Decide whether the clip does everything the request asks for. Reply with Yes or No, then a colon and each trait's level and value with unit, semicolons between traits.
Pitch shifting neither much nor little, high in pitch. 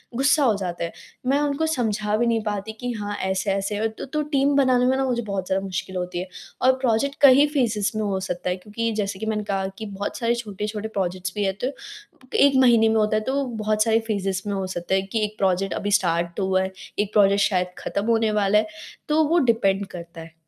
Yes: average, 3.4 semitones; high, 210 Hz